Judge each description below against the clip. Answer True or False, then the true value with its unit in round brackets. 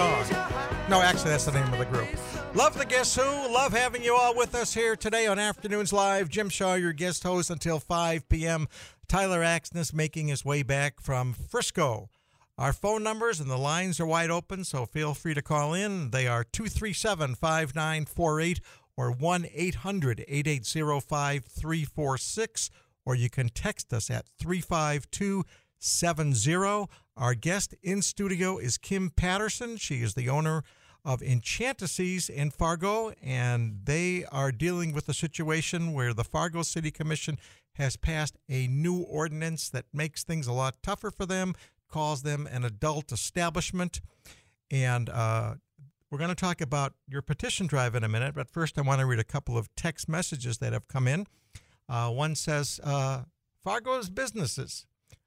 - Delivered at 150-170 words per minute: True (160 wpm)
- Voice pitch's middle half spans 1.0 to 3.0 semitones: False (5.4 semitones)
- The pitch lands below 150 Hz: False (155 Hz)